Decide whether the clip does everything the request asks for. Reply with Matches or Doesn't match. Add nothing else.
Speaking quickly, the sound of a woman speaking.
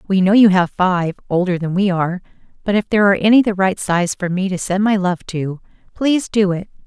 Matches